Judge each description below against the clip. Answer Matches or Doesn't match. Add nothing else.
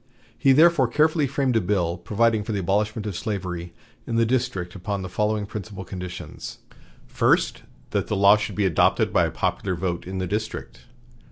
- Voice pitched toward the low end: Matches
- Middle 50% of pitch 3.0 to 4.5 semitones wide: Matches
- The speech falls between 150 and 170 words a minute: Doesn't match